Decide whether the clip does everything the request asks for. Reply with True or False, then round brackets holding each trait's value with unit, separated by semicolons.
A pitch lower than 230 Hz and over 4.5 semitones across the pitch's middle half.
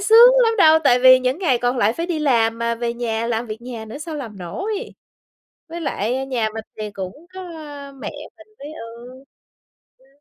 False (245 Hz; 5.5 semitones)